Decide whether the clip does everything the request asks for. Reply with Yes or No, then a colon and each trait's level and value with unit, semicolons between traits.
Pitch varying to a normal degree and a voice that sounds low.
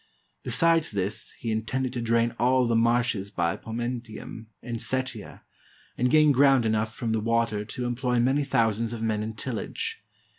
No: narrow, 2.2 semitones; low, 115 Hz